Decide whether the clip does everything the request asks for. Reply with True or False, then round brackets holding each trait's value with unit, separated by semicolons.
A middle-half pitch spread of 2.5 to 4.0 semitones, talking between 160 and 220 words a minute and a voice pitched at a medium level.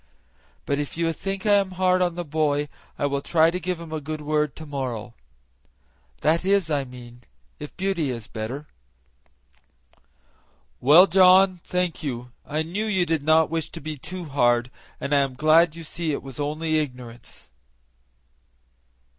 True (3.7 semitones; 165 wpm; 155 Hz)